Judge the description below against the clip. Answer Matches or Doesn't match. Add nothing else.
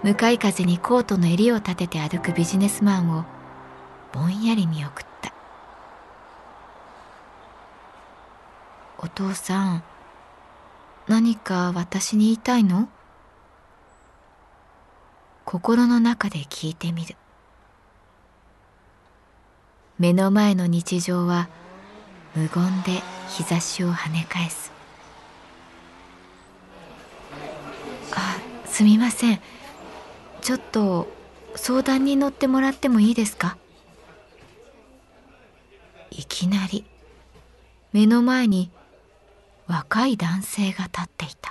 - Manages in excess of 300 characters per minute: Doesn't match